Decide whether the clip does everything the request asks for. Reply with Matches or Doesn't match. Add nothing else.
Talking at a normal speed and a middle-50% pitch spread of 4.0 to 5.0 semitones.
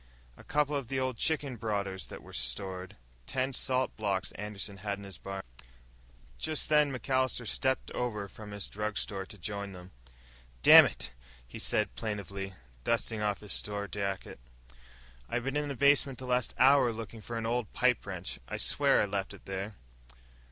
Matches